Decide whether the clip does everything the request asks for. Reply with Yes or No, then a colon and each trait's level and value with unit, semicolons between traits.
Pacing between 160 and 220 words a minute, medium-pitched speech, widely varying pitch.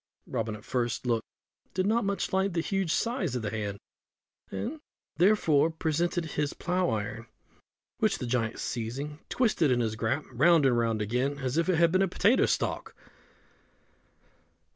Yes: average, 165 wpm; medium, 145 Hz; wide, 7.3 semitones